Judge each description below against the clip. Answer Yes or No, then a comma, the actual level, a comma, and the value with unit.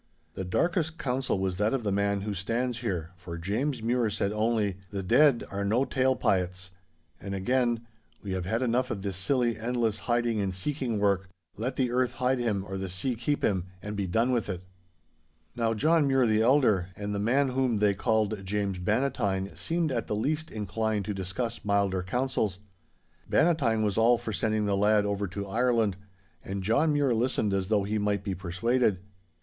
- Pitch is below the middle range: Yes, low, 110 Hz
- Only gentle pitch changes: No, average, 4.1 semitones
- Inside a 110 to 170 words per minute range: No, average, 190 wpm